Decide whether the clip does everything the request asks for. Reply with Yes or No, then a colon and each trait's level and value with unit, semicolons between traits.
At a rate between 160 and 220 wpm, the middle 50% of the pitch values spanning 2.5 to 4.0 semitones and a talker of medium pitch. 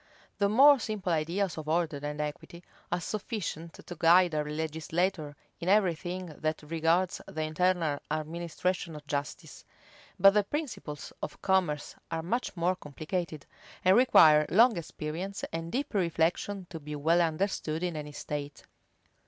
No: average, 145 wpm; average, 3.3 semitones; medium, 170 Hz